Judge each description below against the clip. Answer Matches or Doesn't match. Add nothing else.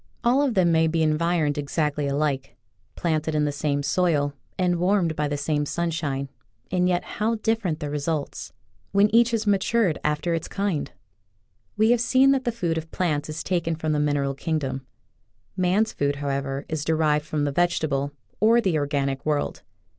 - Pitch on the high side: Doesn't match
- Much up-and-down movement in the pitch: Doesn't match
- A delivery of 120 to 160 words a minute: Doesn't match